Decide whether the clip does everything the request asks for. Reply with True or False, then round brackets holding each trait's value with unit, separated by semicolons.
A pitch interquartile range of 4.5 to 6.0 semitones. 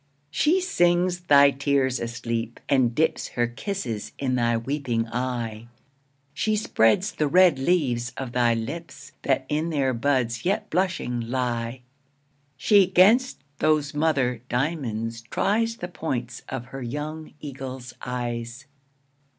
True (5.2 semitones)